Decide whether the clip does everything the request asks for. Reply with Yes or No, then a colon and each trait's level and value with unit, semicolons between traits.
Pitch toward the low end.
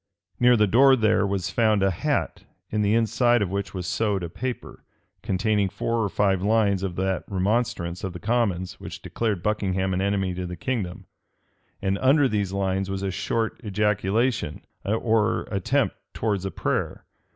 Yes: low, 100 Hz